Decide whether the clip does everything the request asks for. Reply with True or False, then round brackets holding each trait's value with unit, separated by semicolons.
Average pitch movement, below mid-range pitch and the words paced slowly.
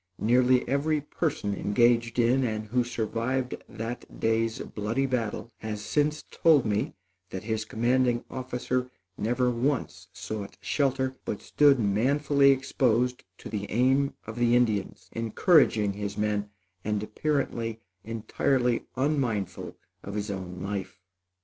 True (3.6 semitones; 120 Hz; 125 wpm)